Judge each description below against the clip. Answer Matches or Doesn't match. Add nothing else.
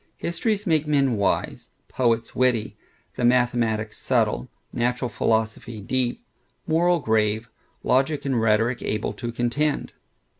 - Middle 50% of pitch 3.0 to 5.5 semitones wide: Matches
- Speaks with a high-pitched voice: Doesn't match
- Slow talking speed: Matches